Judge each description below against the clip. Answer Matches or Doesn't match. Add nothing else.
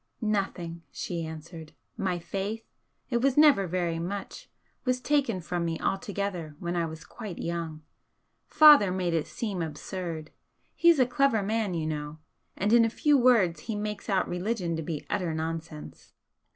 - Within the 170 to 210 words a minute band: Doesn't match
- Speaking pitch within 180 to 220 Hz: Matches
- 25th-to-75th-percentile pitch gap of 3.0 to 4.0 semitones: Doesn't match